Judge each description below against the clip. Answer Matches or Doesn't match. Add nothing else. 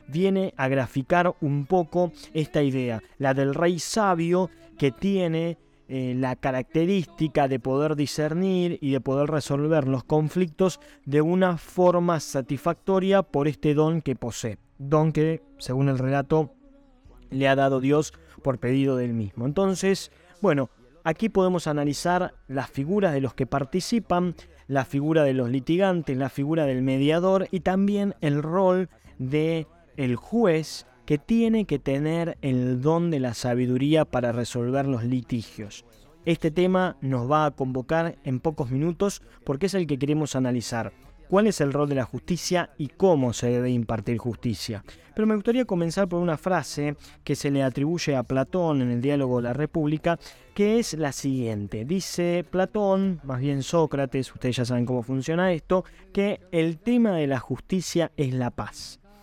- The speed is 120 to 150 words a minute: Doesn't match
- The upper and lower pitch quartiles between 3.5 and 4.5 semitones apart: Doesn't match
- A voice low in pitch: Doesn't match